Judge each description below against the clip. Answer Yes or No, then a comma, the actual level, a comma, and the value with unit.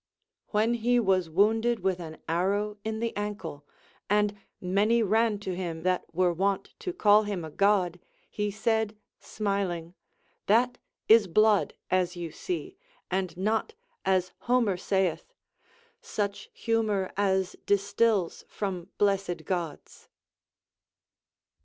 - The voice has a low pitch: No, high, 200 Hz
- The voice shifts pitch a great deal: No, average, 3.2 semitones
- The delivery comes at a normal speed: No, slow, 125 wpm